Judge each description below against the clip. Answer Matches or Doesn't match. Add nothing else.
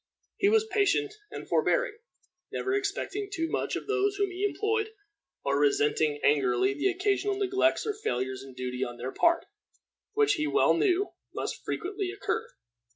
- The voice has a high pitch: Matches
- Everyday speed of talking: Matches